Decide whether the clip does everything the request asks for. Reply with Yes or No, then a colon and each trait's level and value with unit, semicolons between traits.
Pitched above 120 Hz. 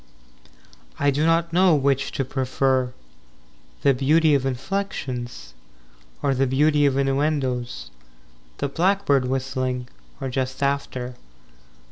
Yes: low, 135 Hz